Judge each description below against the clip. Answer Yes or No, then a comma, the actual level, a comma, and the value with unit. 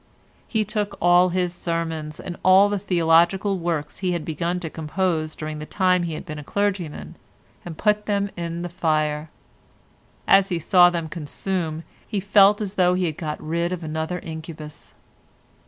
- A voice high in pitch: No, medium, 175 Hz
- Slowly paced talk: No, average, 170 wpm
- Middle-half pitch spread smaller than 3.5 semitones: Yes, average, 2.9 semitones